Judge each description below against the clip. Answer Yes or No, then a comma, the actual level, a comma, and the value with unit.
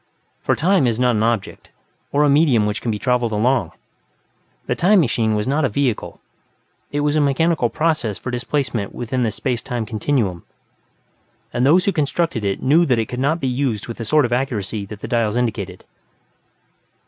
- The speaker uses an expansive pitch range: No, average, 4.6 semitones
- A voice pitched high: No, low, 125 Hz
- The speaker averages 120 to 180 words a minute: No, average, 190 wpm